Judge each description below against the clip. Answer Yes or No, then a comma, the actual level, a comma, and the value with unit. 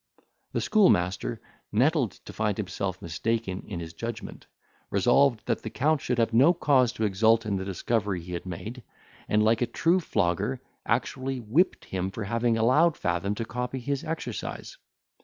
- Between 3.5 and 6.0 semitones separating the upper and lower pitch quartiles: Yes, average, 4.8 semitones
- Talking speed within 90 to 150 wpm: No, average, 165 wpm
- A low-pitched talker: Yes, low, 115 Hz